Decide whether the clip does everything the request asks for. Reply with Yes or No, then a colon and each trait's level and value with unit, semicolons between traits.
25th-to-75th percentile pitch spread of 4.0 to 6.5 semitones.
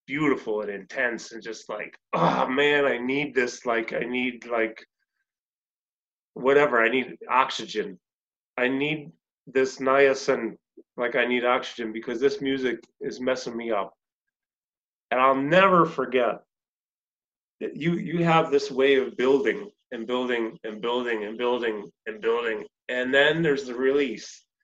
No: average, 3.0 semitones